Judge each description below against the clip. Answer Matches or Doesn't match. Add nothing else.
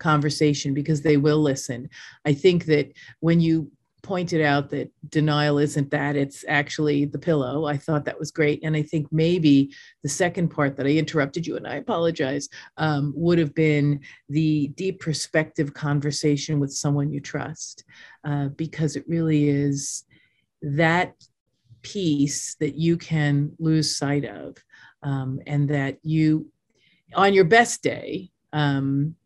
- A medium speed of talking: Matches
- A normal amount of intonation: Doesn't match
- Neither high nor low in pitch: Matches